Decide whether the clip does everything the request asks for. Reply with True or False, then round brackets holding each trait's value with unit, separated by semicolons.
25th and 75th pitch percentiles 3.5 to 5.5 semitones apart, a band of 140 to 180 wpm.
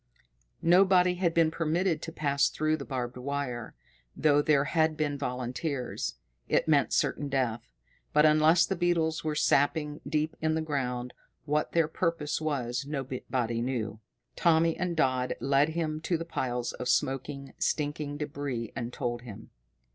True (3.8 semitones; 150 wpm)